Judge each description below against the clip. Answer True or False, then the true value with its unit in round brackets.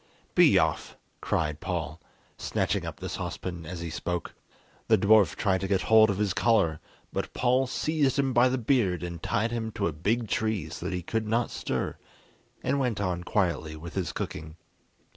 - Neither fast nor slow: True (185 wpm)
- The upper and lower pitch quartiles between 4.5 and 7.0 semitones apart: True (5.1 semitones)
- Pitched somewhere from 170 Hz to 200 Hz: False (100 Hz)